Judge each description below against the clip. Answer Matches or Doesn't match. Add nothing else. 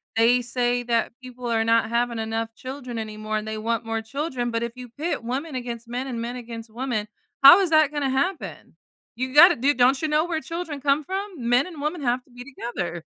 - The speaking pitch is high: Matches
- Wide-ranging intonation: Doesn't match